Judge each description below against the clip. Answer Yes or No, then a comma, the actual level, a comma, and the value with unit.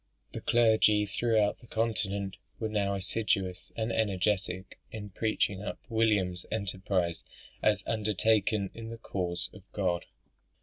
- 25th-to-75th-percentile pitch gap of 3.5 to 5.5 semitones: No, average, 2.7 semitones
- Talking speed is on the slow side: Yes, slow, 125 wpm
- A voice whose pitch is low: Yes, low, 105 Hz